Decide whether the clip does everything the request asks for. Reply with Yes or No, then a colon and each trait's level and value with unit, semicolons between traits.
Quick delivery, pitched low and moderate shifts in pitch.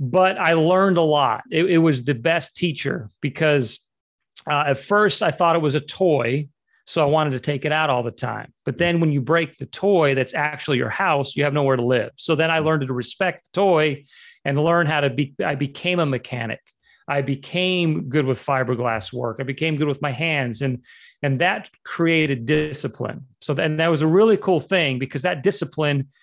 No: fast, 210 wpm; medium, 150 Hz; average, 3.4 semitones